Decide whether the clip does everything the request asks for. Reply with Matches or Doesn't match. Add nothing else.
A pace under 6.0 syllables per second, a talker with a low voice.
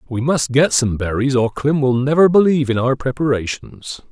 Matches